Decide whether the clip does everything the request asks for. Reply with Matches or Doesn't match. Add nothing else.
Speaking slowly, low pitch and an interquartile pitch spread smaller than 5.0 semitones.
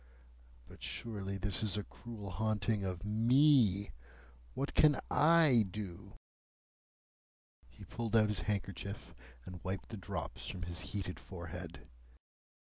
Matches